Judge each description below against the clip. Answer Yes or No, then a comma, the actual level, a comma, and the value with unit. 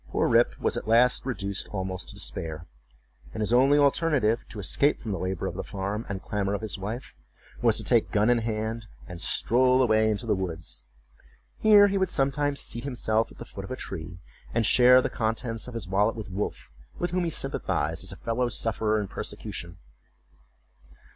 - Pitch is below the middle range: Yes, low, 110 Hz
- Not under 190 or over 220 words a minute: Yes, average, 195 wpm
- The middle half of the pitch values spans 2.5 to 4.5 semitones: Yes, average, 4.2 semitones